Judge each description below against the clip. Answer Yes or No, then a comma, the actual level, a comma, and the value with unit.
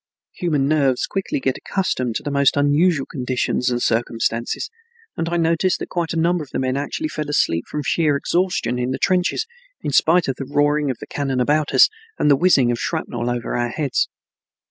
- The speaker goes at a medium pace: Yes, average, 195 wpm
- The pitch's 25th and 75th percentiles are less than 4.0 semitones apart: No, average, 4.7 semitones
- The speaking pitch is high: No, medium, 145 Hz